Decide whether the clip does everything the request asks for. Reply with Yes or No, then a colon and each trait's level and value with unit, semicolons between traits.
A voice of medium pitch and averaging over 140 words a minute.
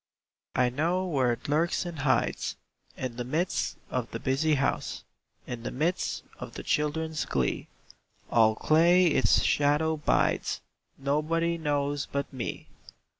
No: medium, 145 Hz; slow, 135 wpm